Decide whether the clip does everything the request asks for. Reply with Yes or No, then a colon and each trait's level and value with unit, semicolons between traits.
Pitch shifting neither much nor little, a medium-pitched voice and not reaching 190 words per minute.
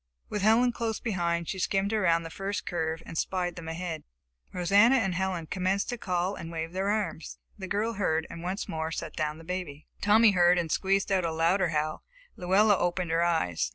No: average, 3.2 semitones; medium, 180 Hz; average, 200 wpm